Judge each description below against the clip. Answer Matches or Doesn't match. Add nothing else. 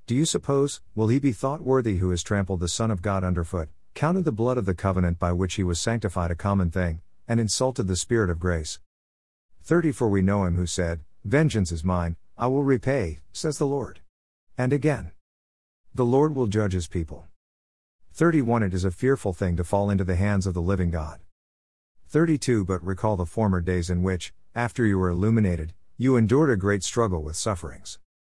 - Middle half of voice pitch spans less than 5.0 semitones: Doesn't match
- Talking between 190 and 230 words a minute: Matches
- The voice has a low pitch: Matches